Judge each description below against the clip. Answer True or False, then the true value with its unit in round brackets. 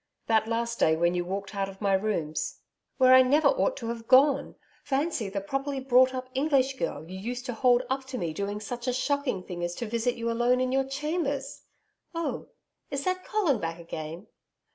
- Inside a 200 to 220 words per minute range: True (205 wpm)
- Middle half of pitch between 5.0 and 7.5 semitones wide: True (5.3 semitones)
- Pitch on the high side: True (245 Hz)